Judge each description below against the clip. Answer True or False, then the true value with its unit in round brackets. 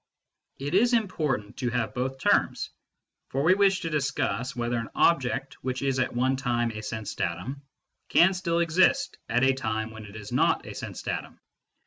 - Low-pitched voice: True (130 Hz)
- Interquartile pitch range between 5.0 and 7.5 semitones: True (5.3 semitones)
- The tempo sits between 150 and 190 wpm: True (180 wpm)